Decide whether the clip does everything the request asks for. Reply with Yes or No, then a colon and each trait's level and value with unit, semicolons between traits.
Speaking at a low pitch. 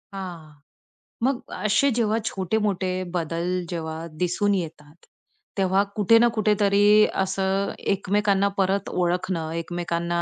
No: high, 190 Hz